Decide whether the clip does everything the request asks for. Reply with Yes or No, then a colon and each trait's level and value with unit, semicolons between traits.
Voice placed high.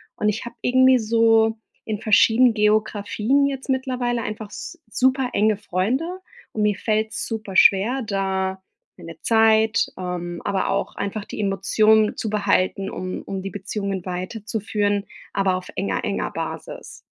Yes: high, 215 Hz